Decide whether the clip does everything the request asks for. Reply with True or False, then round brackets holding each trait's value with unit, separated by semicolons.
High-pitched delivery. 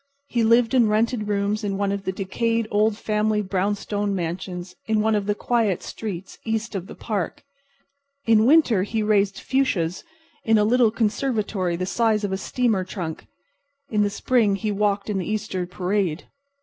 True (210 Hz)